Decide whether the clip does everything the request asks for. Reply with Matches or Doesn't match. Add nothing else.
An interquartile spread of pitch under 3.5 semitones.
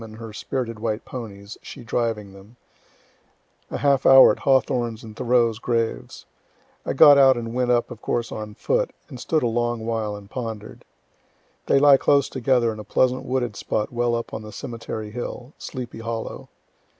Matches